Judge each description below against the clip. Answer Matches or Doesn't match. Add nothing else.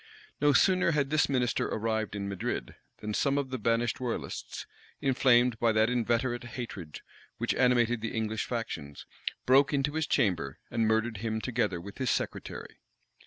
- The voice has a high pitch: Doesn't match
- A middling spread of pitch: Matches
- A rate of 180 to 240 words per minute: Doesn't match